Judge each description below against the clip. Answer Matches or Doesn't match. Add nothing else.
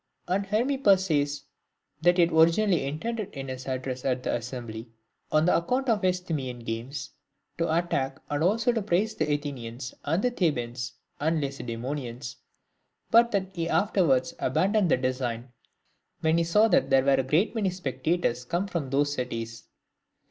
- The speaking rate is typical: Matches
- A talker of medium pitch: Matches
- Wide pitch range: Matches